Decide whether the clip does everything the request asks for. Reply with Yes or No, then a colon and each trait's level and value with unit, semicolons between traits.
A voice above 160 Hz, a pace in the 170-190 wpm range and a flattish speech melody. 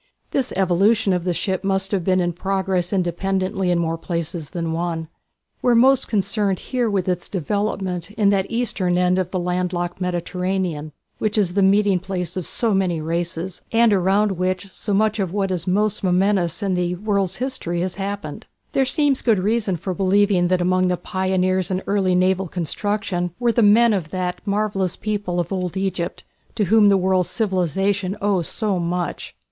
Yes: high, 190 Hz; average, 180 wpm; narrow, 2.3 semitones